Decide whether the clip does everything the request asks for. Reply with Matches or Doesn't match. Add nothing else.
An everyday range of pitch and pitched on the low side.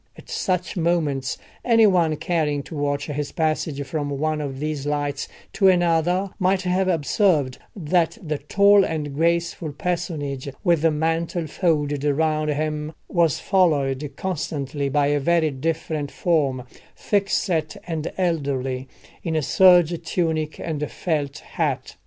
Doesn't match